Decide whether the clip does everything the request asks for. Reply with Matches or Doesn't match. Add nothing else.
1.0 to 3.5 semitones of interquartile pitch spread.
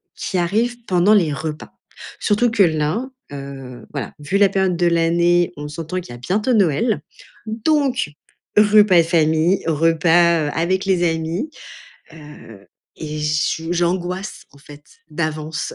Doesn't match